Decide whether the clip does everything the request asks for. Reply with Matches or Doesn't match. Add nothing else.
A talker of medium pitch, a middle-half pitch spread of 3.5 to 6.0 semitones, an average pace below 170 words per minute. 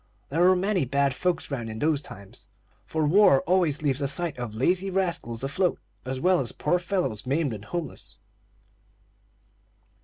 Matches